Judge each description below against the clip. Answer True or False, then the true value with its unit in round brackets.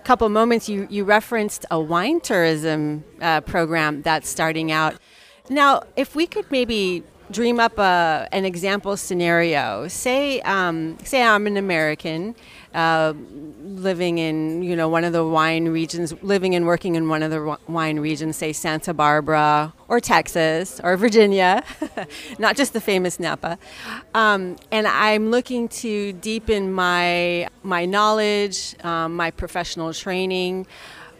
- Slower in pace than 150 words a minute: True (140 wpm)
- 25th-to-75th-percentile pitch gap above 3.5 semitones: True (4.7 semitones)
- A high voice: False (180 Hz)